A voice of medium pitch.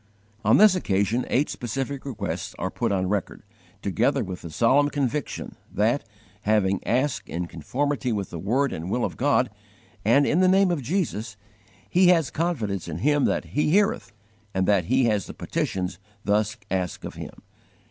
No: low, 120 Hz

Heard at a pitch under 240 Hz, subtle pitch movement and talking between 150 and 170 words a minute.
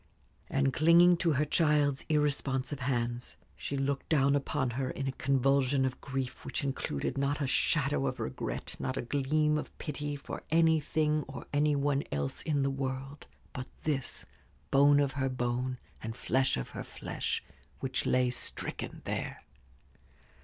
Yes: medium, 140 Hz; narrow, 2.1 semitones; average, 155 wpm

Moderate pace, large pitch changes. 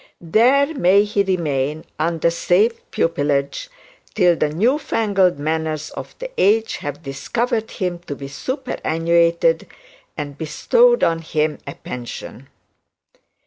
No: slow, 120 wpm; wide, 6.3 semitones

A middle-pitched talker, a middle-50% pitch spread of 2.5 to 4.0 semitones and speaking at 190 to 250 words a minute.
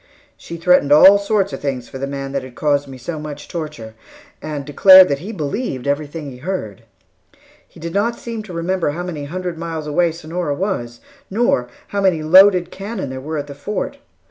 No: medium, 160 Hz; average, 4.7 semitones; average, 195 wpm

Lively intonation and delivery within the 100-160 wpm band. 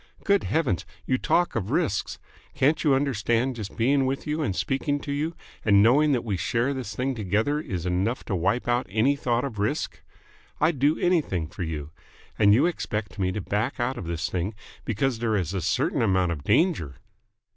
No: wide, 6.4 semitones; average, 200 wpm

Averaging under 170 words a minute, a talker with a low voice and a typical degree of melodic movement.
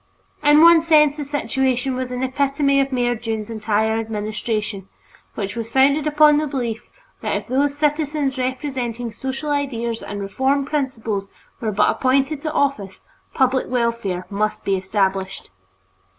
No: average, 145 wpm; very high, 255 Hz; average, 4.3 semitones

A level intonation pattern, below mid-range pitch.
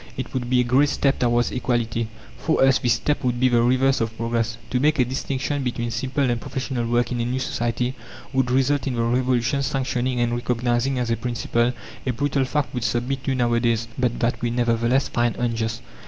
Yes: narrow, 1.8 semitones; low, 125 Hz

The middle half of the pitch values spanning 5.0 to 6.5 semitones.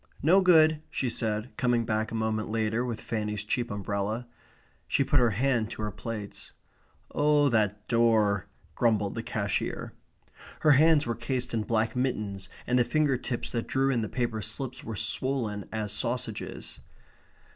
No: average, 3.2 semitones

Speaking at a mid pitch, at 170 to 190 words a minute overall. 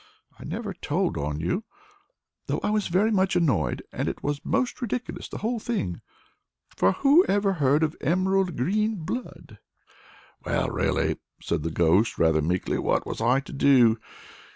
No: medium, 160 Hz; average, 160 wpm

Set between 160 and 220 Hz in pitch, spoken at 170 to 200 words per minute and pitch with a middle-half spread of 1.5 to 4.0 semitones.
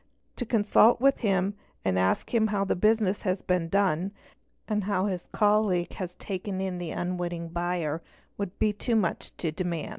Yes: high, 190 Hz; average, 175 wpm; average, 3.1 semitones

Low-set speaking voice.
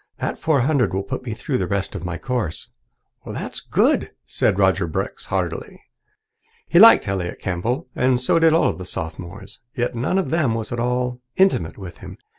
Yes: low, 120 Hz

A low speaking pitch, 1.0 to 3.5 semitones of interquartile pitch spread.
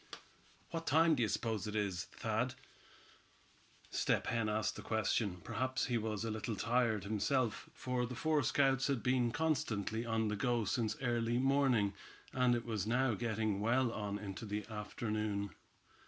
Yes: low, 115 Hz; average, 3.1 semitones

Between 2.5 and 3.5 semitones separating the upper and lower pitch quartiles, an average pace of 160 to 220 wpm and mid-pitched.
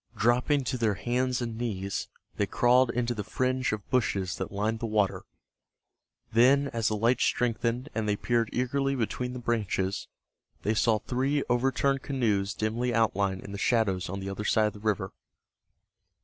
No: average, 3.1 semitones; average, 170 wpm; low, 115 Hz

